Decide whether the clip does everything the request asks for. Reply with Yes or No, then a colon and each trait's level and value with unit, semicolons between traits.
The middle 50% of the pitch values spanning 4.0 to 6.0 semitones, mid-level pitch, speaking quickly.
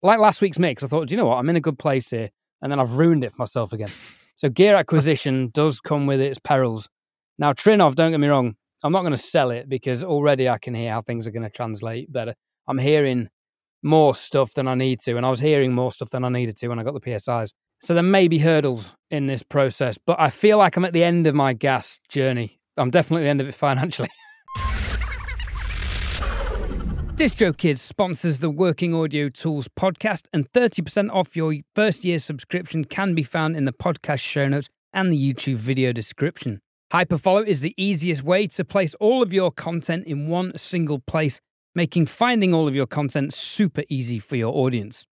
Yes: wide, 5.4 semitones; medium, 145 Hz; fast, 215 wpm